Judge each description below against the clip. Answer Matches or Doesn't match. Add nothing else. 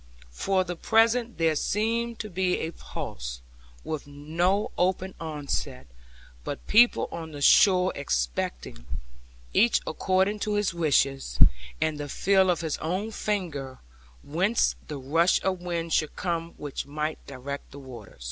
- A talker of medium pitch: Matches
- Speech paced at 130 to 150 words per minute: Matches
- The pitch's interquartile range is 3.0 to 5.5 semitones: Matches